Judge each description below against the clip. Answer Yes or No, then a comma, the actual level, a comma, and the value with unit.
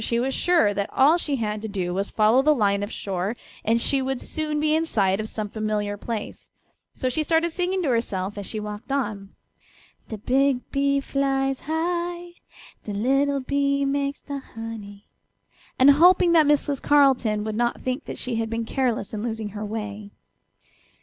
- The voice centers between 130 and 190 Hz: No, high, 245 Hz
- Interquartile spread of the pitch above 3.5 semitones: Yes, average, 5.0 semitones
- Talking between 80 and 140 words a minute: No, average, 185 wpm